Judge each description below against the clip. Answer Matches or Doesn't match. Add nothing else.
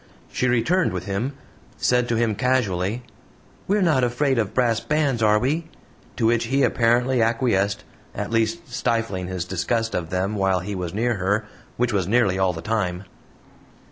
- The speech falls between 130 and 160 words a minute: Doesn't match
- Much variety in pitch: Doesn't match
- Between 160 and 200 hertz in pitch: Doesn't match